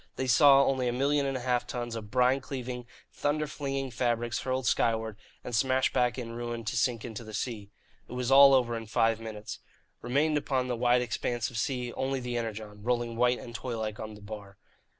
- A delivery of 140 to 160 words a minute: No, fast, 205 wpm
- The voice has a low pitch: Yes, low, 120 Hz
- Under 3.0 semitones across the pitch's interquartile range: Yes, narrow, 2.4 semitones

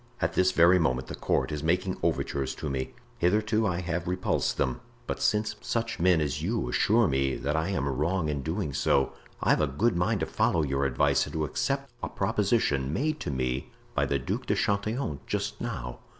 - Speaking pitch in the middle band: No, very low, 85 Hz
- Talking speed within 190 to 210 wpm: Yes, average, 200 wpm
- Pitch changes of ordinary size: No, wide, 6.6 semitones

